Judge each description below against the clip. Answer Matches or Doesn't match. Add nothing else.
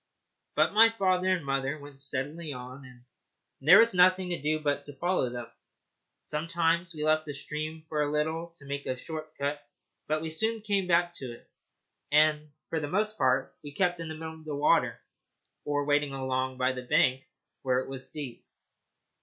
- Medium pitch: Matches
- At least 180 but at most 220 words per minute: Matches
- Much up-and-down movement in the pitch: Doesn't match